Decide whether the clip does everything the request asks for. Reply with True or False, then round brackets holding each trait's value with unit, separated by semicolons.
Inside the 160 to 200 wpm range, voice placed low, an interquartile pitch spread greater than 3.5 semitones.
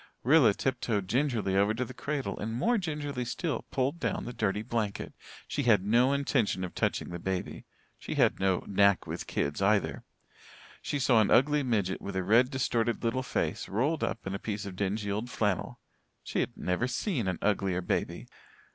True (185 wpm; 115 Hz; 4.6 semitones)